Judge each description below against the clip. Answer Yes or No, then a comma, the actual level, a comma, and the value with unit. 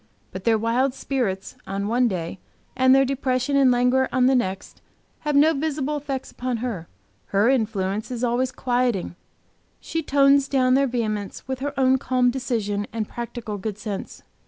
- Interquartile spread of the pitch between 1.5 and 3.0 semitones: No, average, 3.7 semitones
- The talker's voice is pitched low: No, very high, 250 Hz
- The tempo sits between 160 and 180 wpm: Yes, average, 165 wpm